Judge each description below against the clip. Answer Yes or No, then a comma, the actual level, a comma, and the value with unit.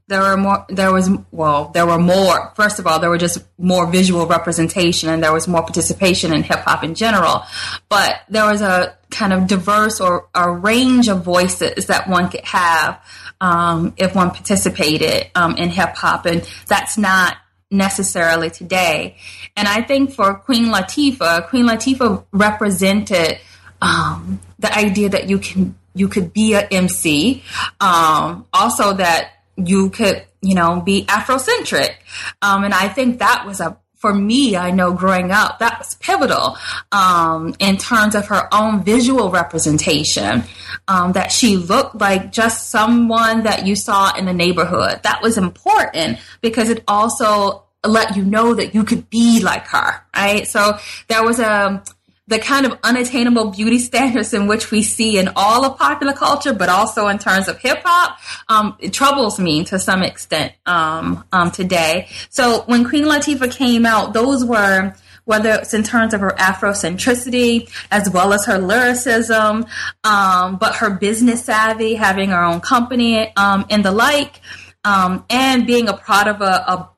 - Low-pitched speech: No, high, 205 Hz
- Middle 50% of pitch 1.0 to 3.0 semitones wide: No, average, 3.7 semitones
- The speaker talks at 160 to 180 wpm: Yes, average, 170 wpm